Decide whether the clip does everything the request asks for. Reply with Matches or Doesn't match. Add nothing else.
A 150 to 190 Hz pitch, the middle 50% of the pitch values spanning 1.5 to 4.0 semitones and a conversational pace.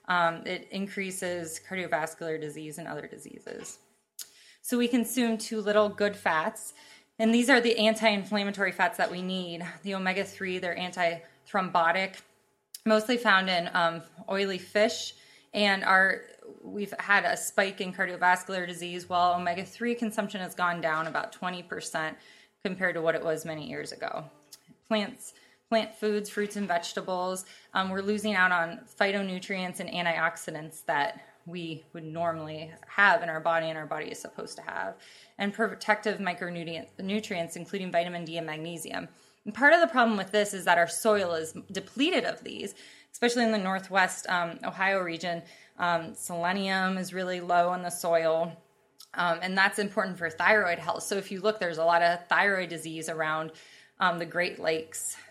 Matches